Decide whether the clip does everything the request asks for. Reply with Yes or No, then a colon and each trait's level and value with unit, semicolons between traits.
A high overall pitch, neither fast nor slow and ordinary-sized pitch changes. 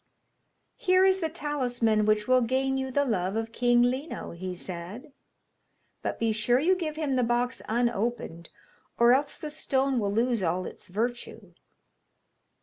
Yes: high, 245 Hz; average, 155 wpm; average, 4.1 semitones